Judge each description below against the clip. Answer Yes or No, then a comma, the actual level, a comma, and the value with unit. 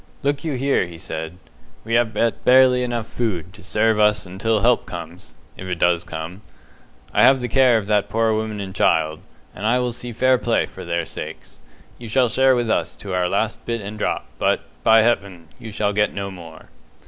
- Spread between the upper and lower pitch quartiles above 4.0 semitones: Yes, average, 4.6 semitones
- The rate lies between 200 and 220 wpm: Yes, fast, 205 wpm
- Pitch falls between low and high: No, low, 110 Hz